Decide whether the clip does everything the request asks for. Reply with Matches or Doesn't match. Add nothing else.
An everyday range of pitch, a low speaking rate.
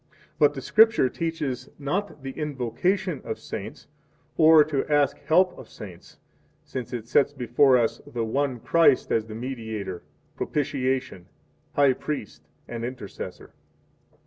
Matches